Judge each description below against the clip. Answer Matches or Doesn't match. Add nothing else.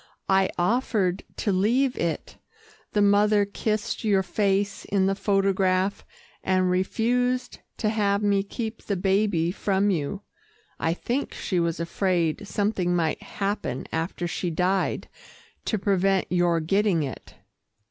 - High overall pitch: Matches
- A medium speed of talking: Doesn't match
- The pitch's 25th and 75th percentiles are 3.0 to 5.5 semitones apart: Doesn't match